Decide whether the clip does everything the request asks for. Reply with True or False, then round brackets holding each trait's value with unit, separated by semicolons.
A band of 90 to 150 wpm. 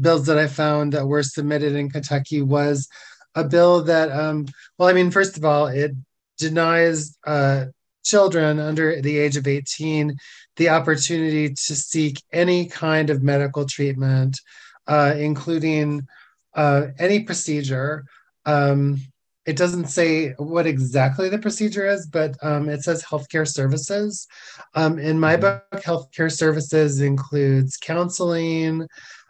True (135 wpm)